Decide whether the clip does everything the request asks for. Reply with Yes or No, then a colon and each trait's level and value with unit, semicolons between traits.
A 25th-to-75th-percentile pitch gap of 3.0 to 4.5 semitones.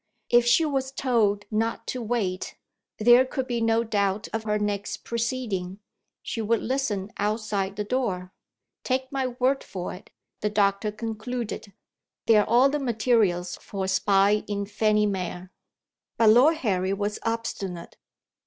Yes: average, 3.3 semitones